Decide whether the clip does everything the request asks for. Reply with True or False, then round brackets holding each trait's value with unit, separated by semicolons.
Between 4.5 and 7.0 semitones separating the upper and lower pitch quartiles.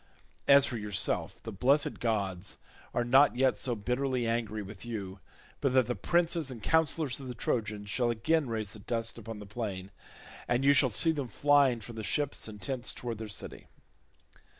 False (4.1 semitones)